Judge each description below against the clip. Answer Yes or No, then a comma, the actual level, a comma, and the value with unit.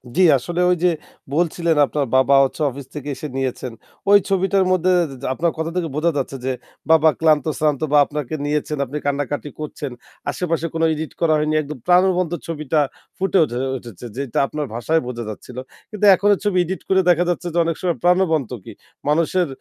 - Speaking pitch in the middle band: Yes, medium, 155 Hz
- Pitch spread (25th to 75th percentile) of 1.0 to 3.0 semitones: No, average, 3.7 semitones